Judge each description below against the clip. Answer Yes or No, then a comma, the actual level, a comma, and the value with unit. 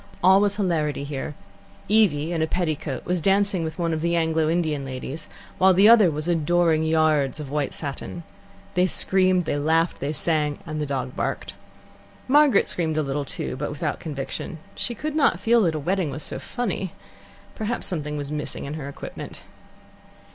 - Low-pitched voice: No, medium, 160 Hz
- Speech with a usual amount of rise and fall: Yes, average, 3.9 semitones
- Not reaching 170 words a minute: No, average, 180 wpm